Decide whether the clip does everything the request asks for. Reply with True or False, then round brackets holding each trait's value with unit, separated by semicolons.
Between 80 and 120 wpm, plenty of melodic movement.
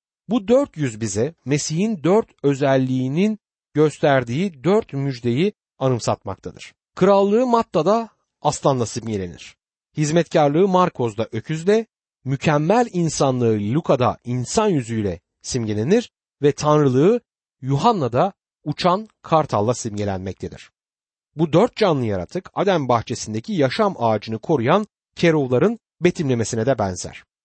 True (95 wpm; 7.4 semitones)